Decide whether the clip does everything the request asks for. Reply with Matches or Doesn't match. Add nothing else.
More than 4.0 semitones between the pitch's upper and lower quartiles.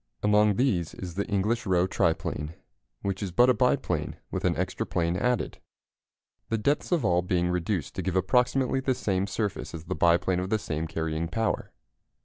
Matches